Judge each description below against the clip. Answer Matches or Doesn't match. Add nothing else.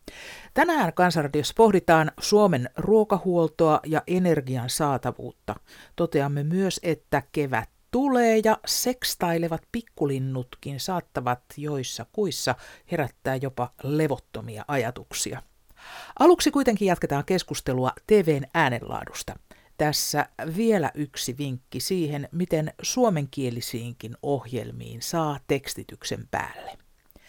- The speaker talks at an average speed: Doesn't match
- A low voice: Doesn't match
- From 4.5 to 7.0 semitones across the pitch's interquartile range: Matches